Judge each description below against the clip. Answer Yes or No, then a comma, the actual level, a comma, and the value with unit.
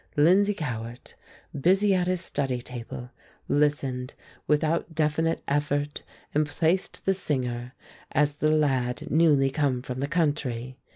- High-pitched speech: No, medium, 145 Hz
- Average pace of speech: No, slow, 125 wpm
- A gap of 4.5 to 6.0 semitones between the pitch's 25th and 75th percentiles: No, average, 4.0 semitones